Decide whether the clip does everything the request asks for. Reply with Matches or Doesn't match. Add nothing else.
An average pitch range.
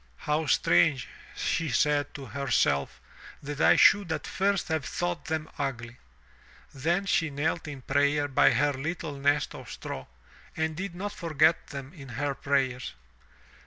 Matches